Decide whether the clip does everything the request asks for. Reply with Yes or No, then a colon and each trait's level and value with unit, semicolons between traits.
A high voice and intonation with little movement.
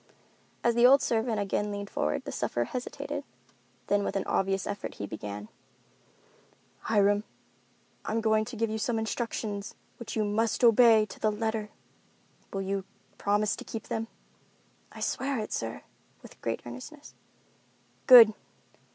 Yes: high, 215 Hz; narrow, 2.1 semitones